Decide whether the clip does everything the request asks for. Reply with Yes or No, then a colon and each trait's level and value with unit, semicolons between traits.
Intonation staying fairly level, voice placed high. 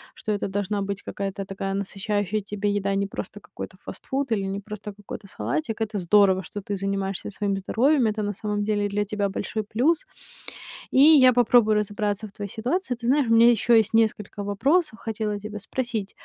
Yes: narrow, 2.2 semitones; high, 210 Hz